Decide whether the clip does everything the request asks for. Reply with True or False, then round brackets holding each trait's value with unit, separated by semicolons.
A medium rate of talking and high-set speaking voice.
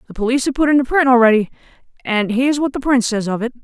False (250 wpm; 250 Hz)